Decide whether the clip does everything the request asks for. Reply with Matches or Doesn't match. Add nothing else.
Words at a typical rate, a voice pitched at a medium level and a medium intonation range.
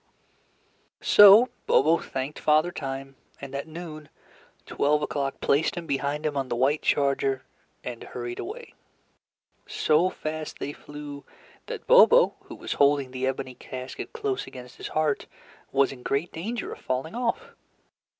Matches